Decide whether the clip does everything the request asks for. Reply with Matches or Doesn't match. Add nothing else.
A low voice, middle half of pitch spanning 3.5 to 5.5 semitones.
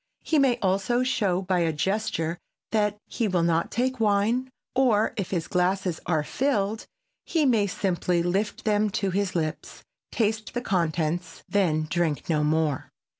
Doesn't match